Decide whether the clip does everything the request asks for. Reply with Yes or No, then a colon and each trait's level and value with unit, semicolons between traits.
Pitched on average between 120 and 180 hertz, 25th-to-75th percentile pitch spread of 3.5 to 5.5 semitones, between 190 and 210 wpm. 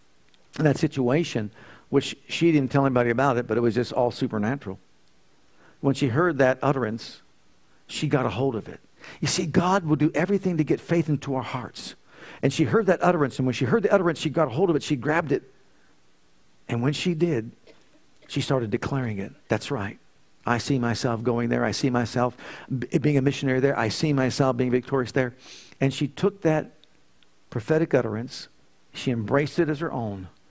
Yes: low, 135 Hz; average, 4.6 semitones; average, 195 wpm